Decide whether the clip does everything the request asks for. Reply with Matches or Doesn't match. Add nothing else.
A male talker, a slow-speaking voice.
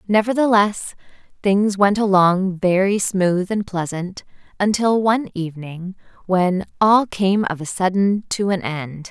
Doesn't match